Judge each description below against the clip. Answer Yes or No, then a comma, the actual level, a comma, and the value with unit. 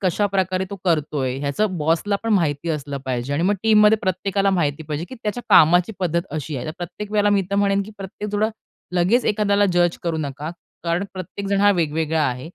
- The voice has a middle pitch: Yes, medium, 180 Hz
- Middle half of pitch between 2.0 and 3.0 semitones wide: No, average, 4.5 semitones